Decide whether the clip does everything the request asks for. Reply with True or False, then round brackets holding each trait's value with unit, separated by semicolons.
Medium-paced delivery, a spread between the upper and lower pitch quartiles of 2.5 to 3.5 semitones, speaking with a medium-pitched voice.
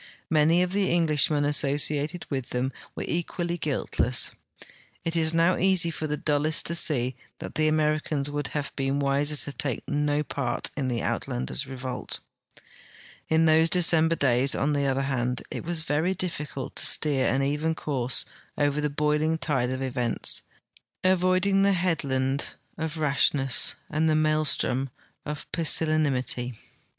True (150 wpm; 2.9 semitones; 150 Hz)